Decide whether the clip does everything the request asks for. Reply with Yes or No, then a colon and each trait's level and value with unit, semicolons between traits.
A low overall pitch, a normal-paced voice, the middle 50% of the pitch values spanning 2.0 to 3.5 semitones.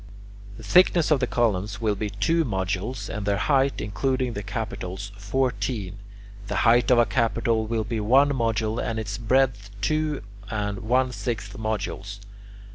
No: low, 110 Hz; average, 155 wpm; average, 3.9 semitones